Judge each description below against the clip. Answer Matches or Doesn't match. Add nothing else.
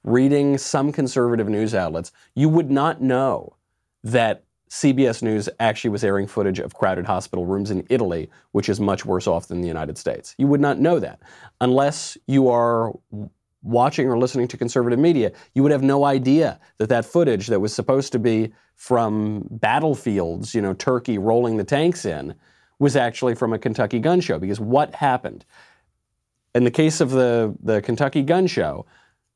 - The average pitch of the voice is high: Doesn't match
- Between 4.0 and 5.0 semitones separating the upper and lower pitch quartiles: Matches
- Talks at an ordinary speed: Matches